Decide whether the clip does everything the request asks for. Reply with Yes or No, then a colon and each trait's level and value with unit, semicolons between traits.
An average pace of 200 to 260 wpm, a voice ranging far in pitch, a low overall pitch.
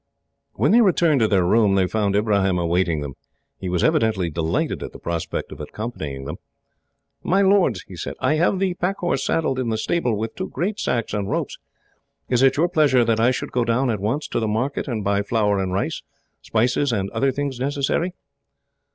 Yes: fast, 205 wpm; wide, 6.4 semitones; low, 115 Hz